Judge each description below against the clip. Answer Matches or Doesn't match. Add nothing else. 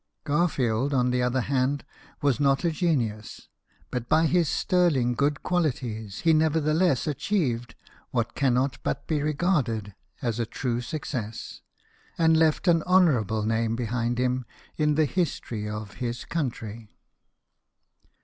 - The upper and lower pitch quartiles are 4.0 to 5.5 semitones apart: Matches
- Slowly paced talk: Matches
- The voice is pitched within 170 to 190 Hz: Doesn't match